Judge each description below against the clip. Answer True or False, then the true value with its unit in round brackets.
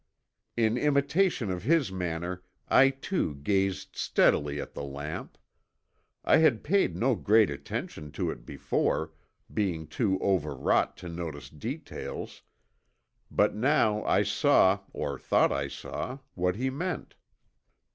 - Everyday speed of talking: False (125 wpm)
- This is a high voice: False (100 Hz)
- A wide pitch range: True (8.4 semitones)